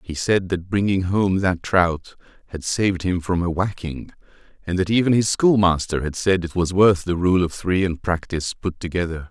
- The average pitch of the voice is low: Yes, very low, 90 Hz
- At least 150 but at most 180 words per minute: No, fast, 205 wpm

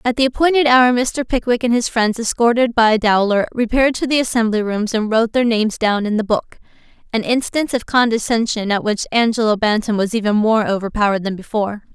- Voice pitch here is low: No, high, 225 Hz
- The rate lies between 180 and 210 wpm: Yes, average, 190 wpm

